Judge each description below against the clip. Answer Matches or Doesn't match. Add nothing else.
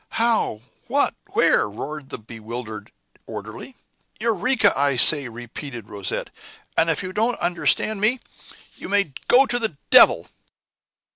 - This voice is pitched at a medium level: Matches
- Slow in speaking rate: Matches